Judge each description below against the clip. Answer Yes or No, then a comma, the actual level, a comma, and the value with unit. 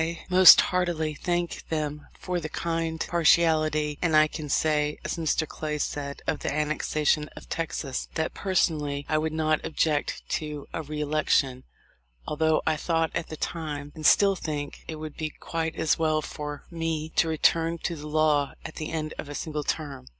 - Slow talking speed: No, average, 180 wpm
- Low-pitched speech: No, medium, 155 Hz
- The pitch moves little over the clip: Yes, narrow, 1.5 semitones